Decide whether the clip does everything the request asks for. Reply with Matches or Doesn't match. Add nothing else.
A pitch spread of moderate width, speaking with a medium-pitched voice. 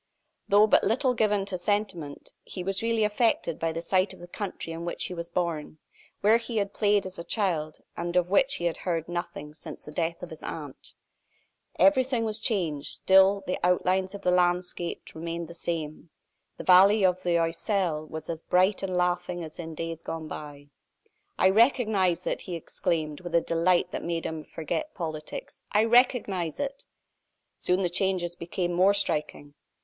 Matches